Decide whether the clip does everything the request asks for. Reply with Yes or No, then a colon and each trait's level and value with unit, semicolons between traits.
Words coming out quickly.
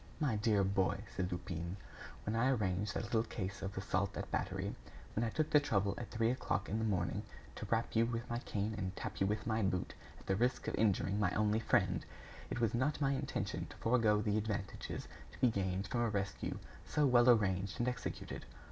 Yes: fast, 210 wpm